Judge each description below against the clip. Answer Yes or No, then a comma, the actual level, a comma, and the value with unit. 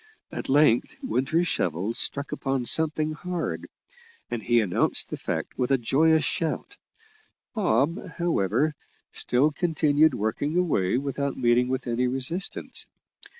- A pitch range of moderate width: Yes, average, 4.7 semitones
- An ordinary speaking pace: No, slow, 125 wpm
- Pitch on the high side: No, medium, 140 Hz